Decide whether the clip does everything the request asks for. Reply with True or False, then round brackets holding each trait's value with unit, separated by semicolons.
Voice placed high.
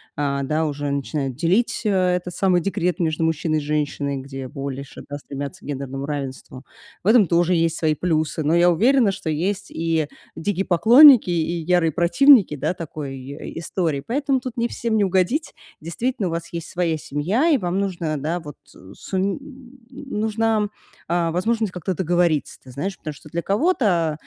False (170 Hz)